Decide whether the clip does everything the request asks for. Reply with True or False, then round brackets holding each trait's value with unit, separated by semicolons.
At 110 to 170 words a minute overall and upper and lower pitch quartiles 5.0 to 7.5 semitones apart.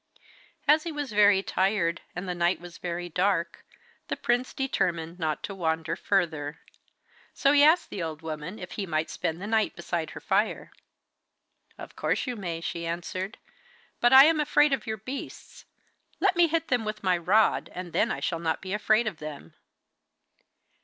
False (180 wpm; 5.5 semitones)